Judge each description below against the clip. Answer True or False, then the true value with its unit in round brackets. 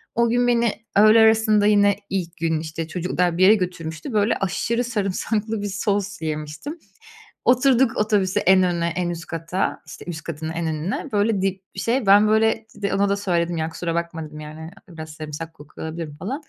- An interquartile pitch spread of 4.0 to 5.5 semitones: True (4.6 semitones)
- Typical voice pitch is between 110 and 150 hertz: False (190 Hz)